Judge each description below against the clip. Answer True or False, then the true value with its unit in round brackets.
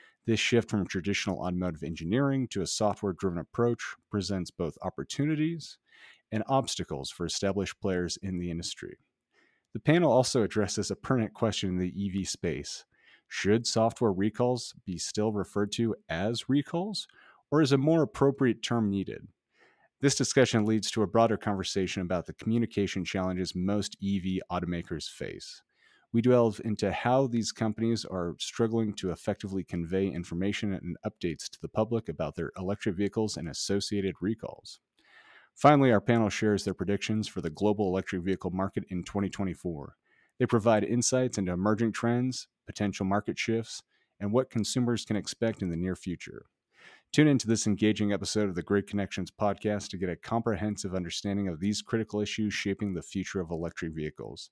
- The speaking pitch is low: True (105 Hz)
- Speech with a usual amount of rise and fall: True (3.3 semitones)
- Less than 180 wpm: True (160 wpm)